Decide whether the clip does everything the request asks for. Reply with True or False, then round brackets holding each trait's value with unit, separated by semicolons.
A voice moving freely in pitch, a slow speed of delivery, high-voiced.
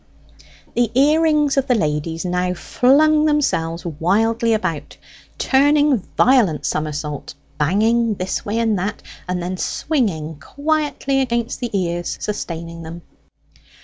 True (8.1 semitones; 120 wpm; 210 Hz)